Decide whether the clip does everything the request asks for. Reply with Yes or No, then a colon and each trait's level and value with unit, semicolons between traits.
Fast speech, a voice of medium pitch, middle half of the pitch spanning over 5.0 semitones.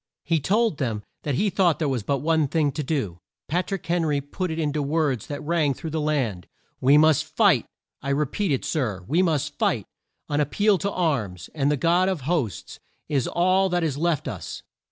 No: fast, 215 wpm; medium, 150 Hz; average, 3.8 semitones